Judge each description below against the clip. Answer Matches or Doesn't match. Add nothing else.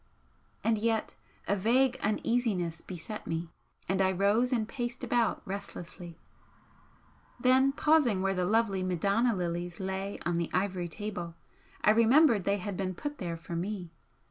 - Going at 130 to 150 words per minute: Matches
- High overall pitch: Matches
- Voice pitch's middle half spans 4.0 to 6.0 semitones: Matches